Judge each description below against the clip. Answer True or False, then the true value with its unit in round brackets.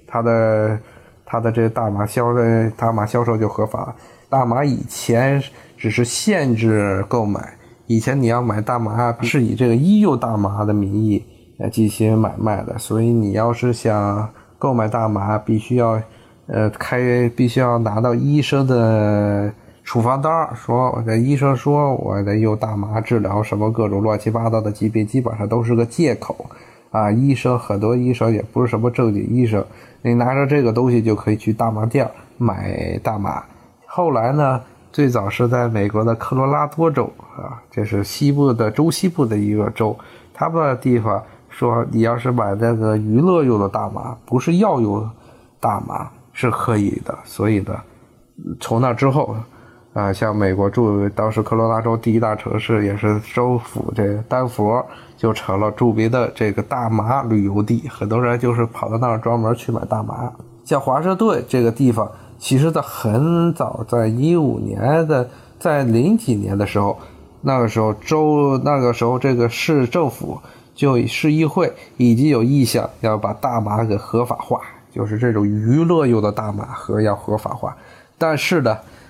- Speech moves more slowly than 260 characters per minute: True (250 characters per minute)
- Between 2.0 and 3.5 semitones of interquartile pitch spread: True (2.6 semitones)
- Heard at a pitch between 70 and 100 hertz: False (115 Hz)